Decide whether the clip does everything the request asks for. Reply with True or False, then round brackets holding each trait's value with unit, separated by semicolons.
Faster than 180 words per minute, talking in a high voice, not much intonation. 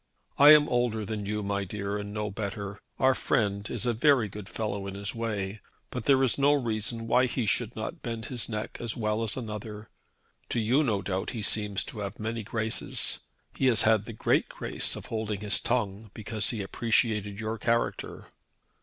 False (195 wpm; 110 Hz; 2.3 semitones)